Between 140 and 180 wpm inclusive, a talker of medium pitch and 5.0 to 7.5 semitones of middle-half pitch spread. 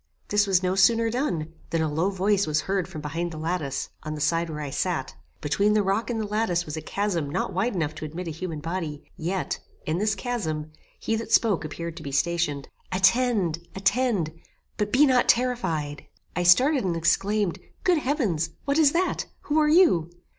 No: average, 195 wpm; medium, 180 Hz; wide, 5.5 semitones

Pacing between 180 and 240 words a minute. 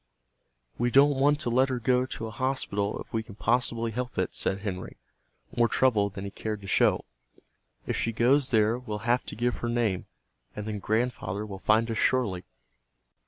Yes: average, 190 wpm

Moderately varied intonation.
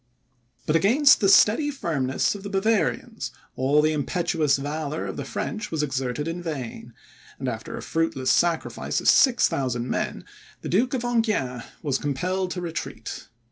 No: wide, 6.7 semitones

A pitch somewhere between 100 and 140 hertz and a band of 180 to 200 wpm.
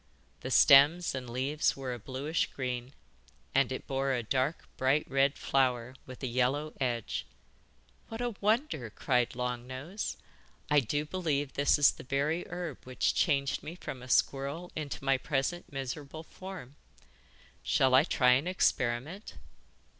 No: low, 135 Hz; average, 150 wpm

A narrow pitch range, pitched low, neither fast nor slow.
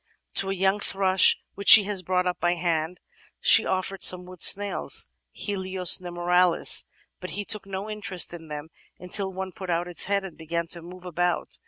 No: narrow, 1.9 semitones; medium, 185 Hz; average, 185 wpm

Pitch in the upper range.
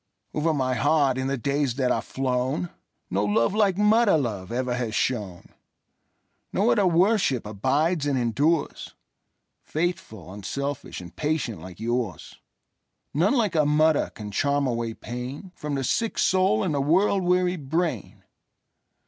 No: medium, 140 Hz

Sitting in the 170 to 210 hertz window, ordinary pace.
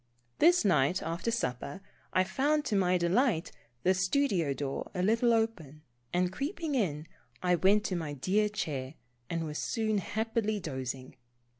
Yes: medium, 185 Hz; average, 150 wpm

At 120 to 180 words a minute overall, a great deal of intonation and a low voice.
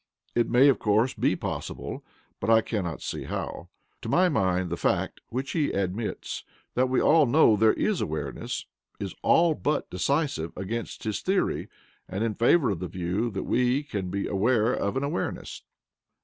Yes: average, 170 wpm; wide, 6.1 semitones; low, 115 Hz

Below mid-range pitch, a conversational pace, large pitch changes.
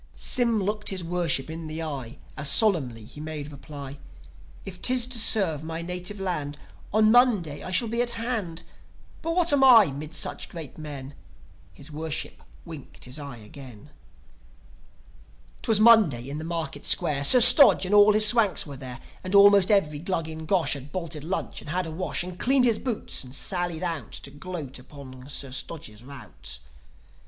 No: medium, 165 Hz; average, 175 wpm; wide, 6.2 semitones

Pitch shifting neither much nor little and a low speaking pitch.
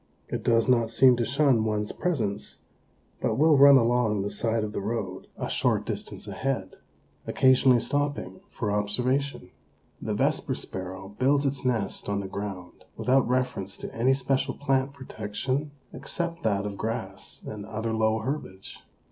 Yes: average, 4.5 semitones; low, 115 Hz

